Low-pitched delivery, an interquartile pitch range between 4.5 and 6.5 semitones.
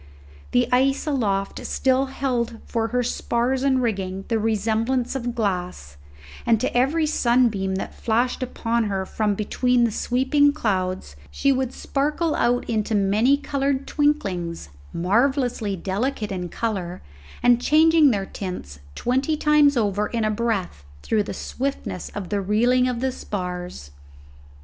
No: high, 235 Hz; average, 5.0 semitones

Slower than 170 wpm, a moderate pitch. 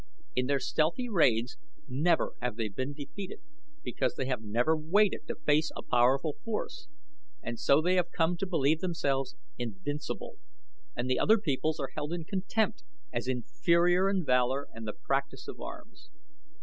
Yes: average, 160 wpm; medium, 145 Hz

